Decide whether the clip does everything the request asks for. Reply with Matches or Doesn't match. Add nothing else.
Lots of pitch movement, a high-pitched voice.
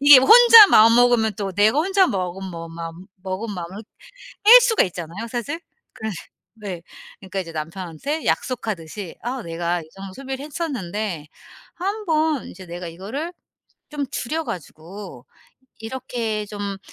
Matches